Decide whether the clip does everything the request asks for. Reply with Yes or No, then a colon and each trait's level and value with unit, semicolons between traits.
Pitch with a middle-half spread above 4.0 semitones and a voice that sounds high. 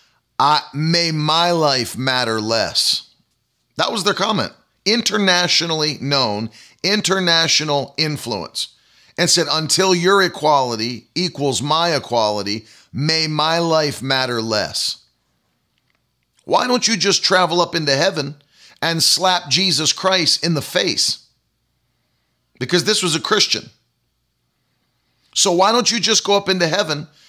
No: average, 4.8 semitones; medium, 160 Hz